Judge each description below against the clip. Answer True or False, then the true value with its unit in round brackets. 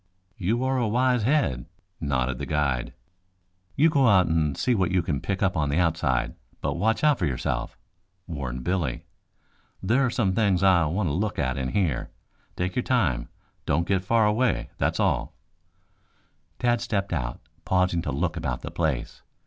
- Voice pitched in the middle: False (90 Hz)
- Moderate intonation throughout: False (7.4 semitones)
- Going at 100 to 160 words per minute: False (175 wpm)